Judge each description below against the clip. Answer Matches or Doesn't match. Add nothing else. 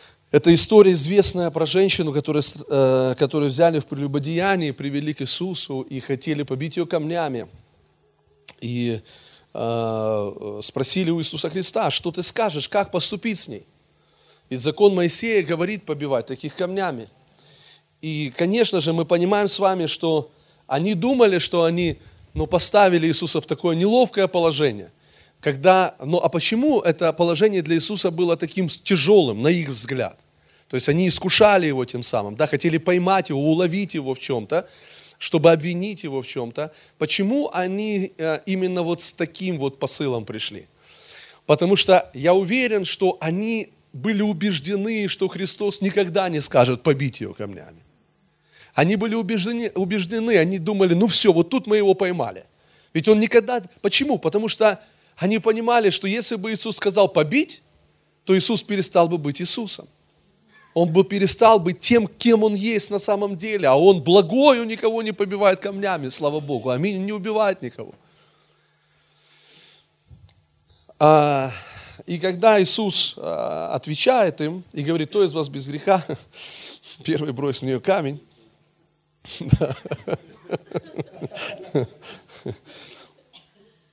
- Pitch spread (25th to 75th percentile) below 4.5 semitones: Doesn't match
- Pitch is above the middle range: Doesn't match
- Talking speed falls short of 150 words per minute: Matches